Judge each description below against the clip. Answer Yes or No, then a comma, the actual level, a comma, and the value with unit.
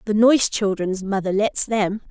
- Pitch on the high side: Yes, high, 205 Hz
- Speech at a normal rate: Yes, average, 170 wpm